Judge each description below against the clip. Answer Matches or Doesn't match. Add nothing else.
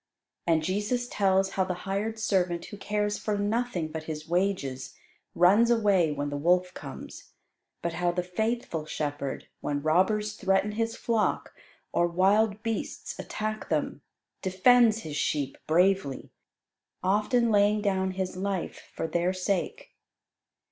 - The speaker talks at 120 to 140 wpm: Matches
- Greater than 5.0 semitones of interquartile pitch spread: Doesn't match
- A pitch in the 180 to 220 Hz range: Matches